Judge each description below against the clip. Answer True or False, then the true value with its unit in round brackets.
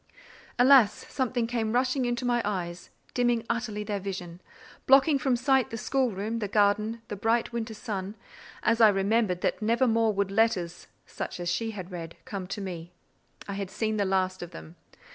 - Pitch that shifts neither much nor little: True (3.6 semitones)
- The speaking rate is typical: True (180 wpm)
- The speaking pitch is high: True (215 Hz)